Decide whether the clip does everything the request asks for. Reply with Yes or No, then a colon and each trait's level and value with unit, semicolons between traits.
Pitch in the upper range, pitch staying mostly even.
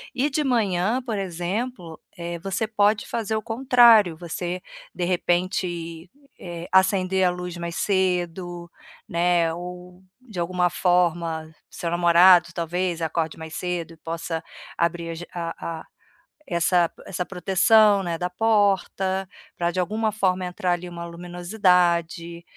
No: medium, 180 Hz; narrow, 2.1 semitones